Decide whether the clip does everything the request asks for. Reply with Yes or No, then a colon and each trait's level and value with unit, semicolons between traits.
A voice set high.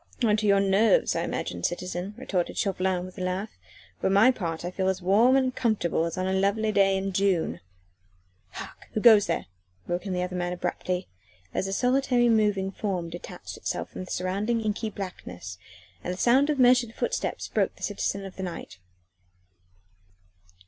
Yes: high, 195 Hz